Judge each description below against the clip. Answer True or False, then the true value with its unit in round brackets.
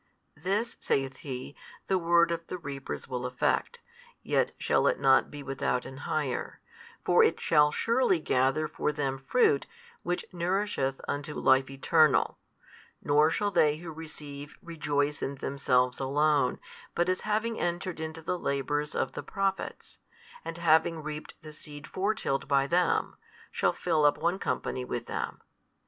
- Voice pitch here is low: False (150 Hz)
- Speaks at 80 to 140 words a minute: False (155 wpm)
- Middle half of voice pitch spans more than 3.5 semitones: True (4.0 semitones)